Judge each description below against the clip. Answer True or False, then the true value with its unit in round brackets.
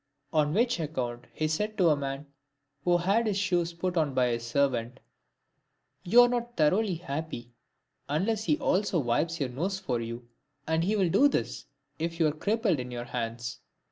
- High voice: False (160 Hz)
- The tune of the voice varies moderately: False (7.2 semitones)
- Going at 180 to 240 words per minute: True (185 wpm)